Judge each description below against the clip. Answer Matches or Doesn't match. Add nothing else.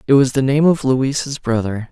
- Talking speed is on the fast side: Matches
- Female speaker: Doesn't match